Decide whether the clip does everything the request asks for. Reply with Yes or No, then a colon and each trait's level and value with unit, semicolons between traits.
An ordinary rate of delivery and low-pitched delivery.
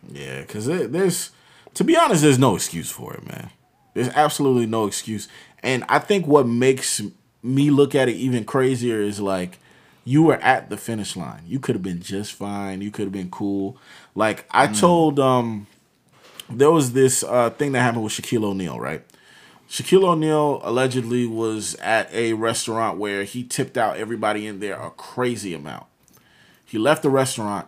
Yes: average, 180 wpm; low, 120 Hz